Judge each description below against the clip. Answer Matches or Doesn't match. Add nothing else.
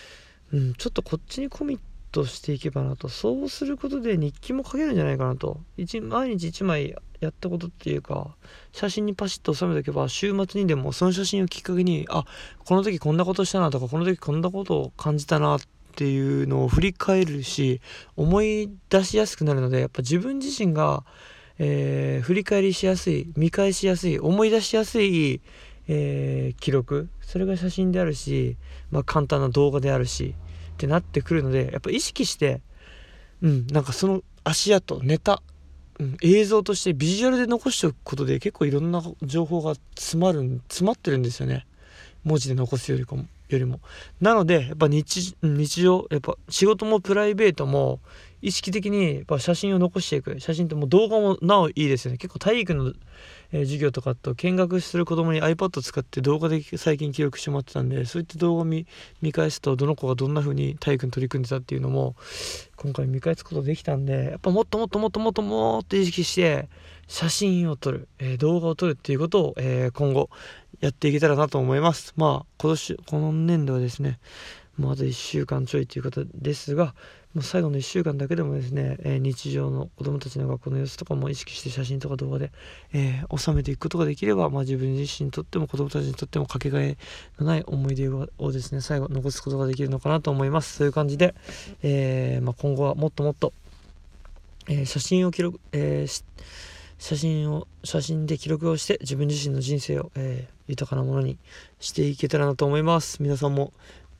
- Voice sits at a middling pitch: Matches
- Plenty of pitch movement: Doesn't match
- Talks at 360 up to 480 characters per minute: Matches